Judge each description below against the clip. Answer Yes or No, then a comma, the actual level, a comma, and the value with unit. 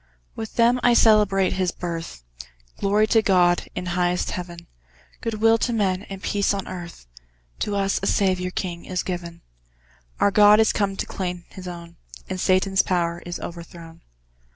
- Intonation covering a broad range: No, average, 2.7 semitones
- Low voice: No, medium, 185 Hz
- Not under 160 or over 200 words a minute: Yes, average, 165 wpm